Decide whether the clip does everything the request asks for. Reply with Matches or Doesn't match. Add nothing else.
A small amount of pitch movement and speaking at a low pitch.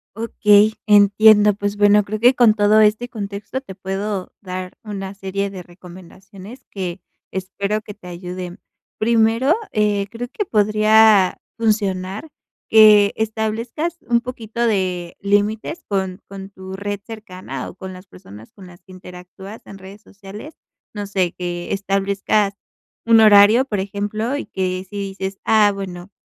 Doesn't match